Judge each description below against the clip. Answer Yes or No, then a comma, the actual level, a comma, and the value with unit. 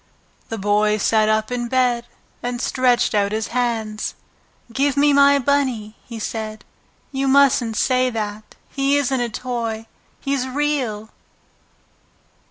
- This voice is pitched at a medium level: No, high, 240 Hz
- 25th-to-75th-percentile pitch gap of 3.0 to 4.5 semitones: Yes, average, 3.6 semitones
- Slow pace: Yes, slow, 130 wpm